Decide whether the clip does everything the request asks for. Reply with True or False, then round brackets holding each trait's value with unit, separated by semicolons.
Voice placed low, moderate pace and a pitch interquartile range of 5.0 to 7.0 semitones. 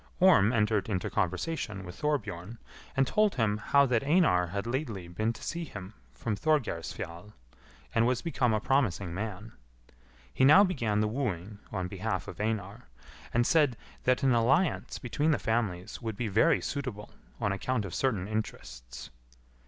True (110 Hz; 160 wpm; 5.3 semitones)